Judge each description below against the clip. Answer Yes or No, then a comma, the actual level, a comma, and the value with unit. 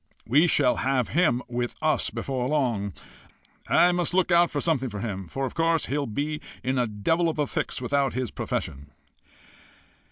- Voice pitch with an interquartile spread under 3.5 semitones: No, average, 4.6 semitones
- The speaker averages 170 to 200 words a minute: Yes, average, 180 wpm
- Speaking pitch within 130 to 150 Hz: Yes, low, 135 Hz